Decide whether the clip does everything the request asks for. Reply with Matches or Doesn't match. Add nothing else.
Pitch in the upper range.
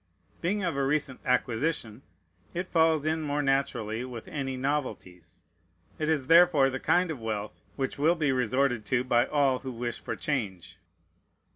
Doesn't match